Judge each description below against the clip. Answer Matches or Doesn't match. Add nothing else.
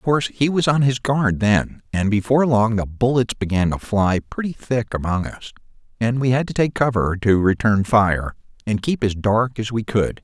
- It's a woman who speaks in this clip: Doesn't match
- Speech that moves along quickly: Matches